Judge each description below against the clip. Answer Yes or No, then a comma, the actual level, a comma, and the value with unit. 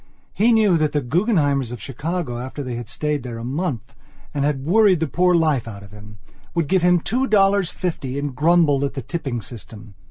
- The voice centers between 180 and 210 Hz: No, medium, 145 Hz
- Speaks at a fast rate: Yes, fast, 210 wpm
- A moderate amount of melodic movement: No, wide, 6.3 semitones